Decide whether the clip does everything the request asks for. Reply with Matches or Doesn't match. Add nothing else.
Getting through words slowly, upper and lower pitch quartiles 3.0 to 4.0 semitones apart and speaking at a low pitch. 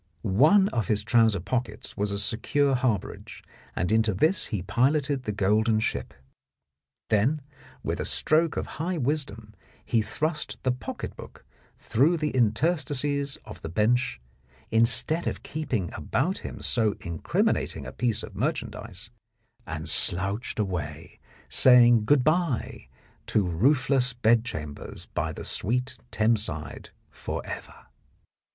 Doesn't match